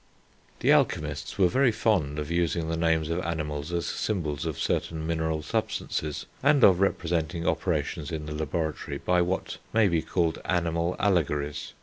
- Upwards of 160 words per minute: No, average, 155 wpm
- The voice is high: No, very low, 85 Hz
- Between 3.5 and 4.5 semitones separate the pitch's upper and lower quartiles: No, narrow, 2.5 semitones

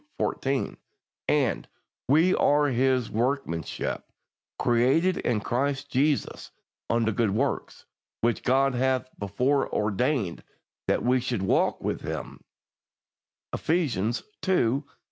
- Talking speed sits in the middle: No, slow, 105 wpm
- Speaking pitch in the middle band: No, low, 130 Hz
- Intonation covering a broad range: No, average, 3.2 semitones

